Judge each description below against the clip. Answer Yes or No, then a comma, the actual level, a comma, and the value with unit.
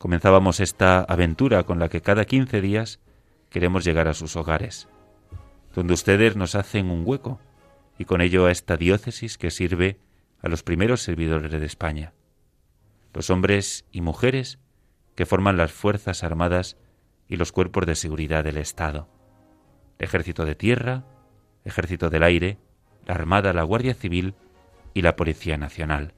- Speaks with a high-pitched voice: No, very low, 90 Hz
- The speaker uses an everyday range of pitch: Yes, average, 3.6 semitones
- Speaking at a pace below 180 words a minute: Yes, average, 155 wpm